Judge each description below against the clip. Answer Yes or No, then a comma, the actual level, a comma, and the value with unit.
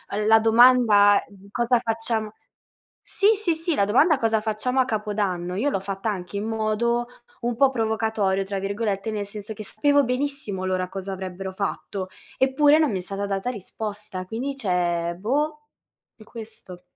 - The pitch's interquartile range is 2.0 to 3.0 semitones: No, average, 3.9 semitones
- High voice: Yes, high, 215 Hz